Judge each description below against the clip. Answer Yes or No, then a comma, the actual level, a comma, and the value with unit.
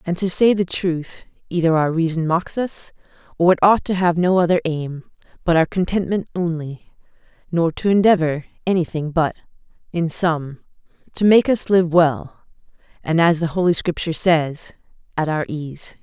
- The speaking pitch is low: No, medium, 170 Hz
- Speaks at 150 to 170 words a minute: Yes, average, 160 wpm